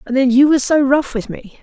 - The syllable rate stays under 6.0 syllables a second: Yes, 5.3 syllables/s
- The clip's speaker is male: No, female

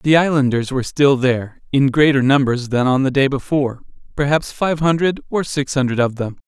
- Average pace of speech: Yes, average, 195 wpm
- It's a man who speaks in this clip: Yes, male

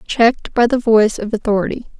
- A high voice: Yes, high, 225 Hz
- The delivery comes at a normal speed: Yes, average, 180 wpm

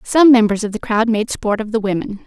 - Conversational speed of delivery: No, fast, 265 wpm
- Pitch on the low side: No, high, 220 Hz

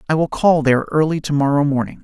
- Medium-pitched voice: Yes, medium, 150 Hz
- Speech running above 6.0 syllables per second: Yes, 6.7 syllables/s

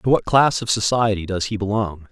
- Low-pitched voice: Yes, low, 105 Hz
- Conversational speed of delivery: No, fast, 225 wpm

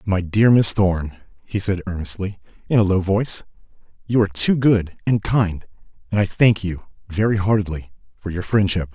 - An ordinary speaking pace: Yes, average, 175 wpm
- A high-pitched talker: No, low, 100 Hz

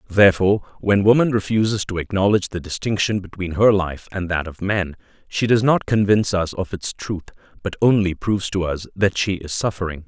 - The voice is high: No, very low, 95 Hz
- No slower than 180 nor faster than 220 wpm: Yes, average, 190 wpm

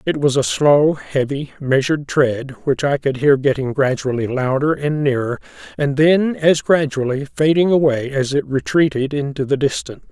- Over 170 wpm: No, average, 165 wpm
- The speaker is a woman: No, male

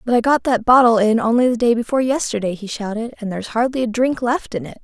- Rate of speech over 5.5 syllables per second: Yes, 6.4 syllables/s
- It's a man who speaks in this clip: No, female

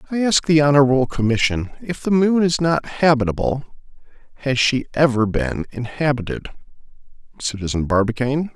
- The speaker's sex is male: Yes, male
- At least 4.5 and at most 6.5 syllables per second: Yes, 5.4 syllables/s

